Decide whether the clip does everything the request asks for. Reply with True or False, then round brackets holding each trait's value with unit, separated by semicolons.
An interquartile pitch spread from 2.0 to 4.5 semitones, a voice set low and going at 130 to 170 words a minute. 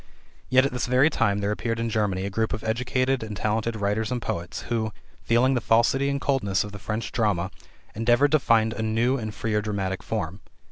False (2.9 semitones; 110 Hz; 205 wpm)